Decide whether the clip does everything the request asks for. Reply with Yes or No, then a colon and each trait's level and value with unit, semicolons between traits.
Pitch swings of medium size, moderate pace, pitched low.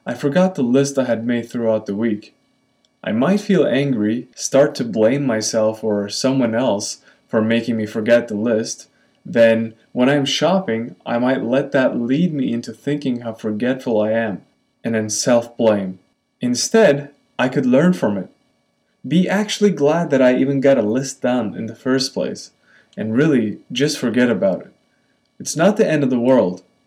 Yes: average, 3.9 semitones; average, 180 wpm; low, 125 Hz